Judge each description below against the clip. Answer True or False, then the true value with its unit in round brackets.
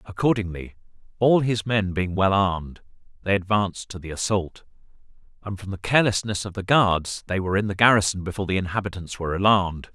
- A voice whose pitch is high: False (100 Hz)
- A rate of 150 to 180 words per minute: True (175 wpm)